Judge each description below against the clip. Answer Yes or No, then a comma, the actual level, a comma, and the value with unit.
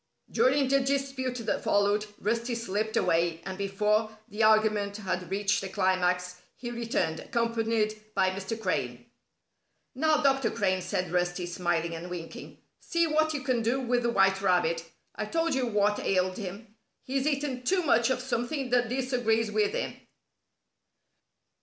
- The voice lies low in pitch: No, high, 215 Hz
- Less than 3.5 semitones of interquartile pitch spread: No, average, 5.0 semitones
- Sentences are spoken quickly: No, average, 155 wpm